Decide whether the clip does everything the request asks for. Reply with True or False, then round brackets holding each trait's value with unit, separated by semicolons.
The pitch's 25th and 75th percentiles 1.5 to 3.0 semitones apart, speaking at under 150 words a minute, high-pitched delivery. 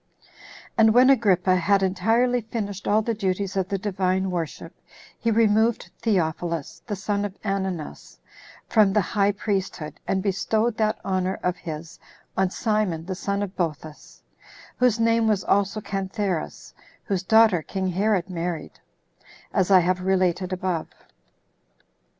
True (2.7 semitones; 140 wpm; 195 Hz)